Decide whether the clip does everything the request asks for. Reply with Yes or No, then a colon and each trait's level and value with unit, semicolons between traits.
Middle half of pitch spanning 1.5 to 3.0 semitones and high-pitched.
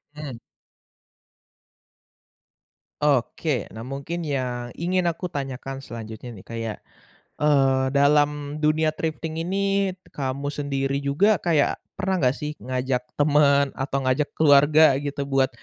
No: average, 2.7 semitones; medium, 140 Hz